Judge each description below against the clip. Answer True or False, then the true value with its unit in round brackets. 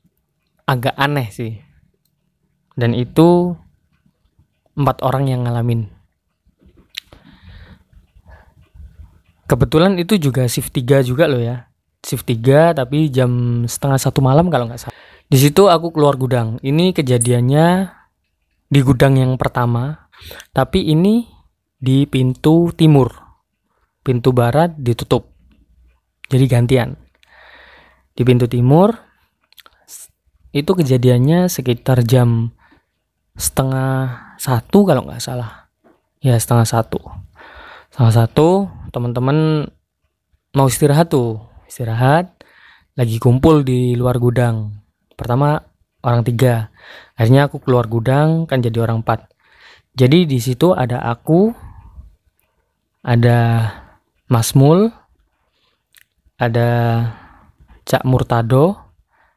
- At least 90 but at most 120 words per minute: True (100 wpm)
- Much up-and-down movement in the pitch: False (3.8 semitones)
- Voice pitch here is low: True (125 Hz)